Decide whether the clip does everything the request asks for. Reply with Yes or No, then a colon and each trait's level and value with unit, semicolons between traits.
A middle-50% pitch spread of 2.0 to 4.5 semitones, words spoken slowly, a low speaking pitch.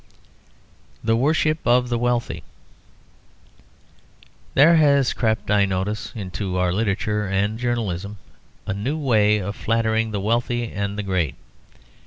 Yes: average, 3.2 semitones; slow, 125 wpm; low, 110 Hz